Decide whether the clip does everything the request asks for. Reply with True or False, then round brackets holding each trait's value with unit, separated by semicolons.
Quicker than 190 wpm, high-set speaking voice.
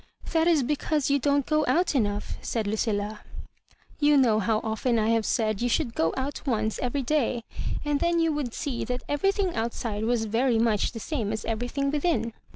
True (200 wpm; 245 Hz)